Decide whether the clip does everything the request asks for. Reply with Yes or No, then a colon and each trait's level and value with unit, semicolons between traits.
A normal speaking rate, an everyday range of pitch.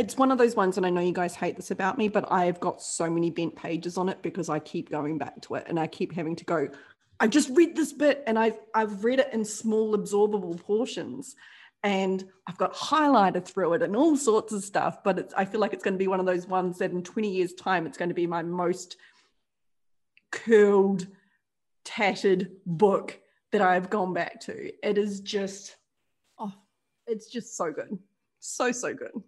No: fast, 215 wpm; average, 3.4 semitones